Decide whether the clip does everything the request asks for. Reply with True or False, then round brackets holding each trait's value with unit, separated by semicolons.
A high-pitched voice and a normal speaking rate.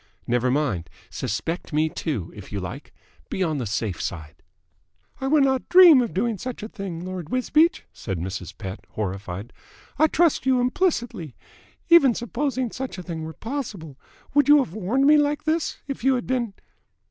True (195 Hz; 175 wpm)